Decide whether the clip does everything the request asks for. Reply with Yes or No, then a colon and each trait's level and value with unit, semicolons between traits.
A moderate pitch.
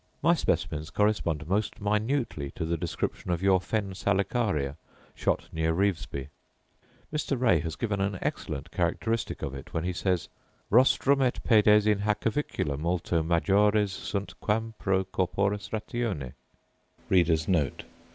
No: low, 100 Hz